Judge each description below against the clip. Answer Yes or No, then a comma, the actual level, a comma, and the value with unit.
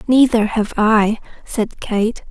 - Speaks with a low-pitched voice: No, high, 220 Hz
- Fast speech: No, slow, 130 wpm